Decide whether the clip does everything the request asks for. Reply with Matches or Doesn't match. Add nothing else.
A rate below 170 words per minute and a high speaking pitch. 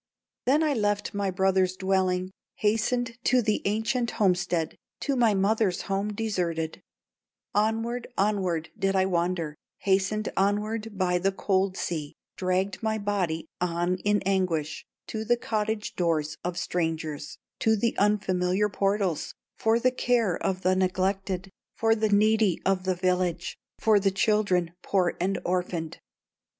Matches